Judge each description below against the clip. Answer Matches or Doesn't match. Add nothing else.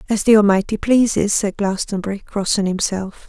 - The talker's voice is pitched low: Doesn't match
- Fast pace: Doesn't match